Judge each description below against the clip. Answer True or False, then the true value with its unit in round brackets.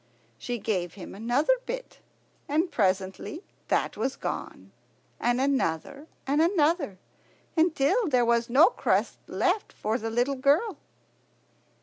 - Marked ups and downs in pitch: True (6.2 semitones)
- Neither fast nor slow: False (120 wpm)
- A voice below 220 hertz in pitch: False (270 Hz)